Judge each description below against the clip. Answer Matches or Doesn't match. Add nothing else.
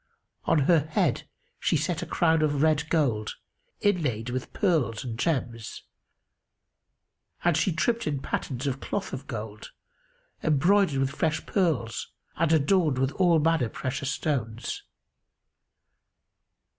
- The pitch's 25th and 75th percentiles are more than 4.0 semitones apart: Matches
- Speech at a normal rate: Doesn't match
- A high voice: Doesn't match